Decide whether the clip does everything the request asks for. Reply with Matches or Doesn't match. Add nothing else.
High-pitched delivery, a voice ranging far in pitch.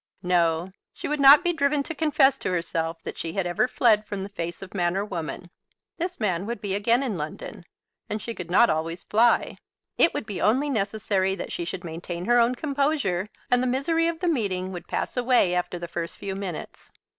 Matches